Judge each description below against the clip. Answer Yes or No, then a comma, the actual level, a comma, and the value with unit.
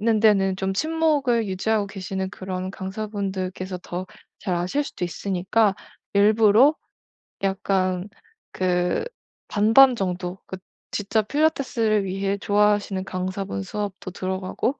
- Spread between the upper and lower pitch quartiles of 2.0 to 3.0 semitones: Yes, narrow, 2.6 semitones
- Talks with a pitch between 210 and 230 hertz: No, high, 195 Hz